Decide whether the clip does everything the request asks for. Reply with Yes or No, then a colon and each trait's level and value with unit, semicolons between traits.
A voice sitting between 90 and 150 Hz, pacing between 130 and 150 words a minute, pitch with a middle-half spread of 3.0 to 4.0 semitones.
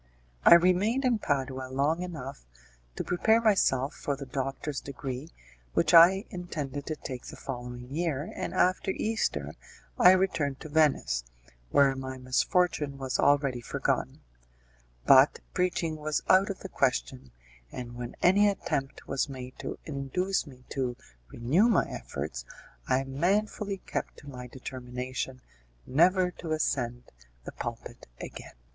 No: medium, 140 Hz; average, 140 wpm; wide, 5.6 semitones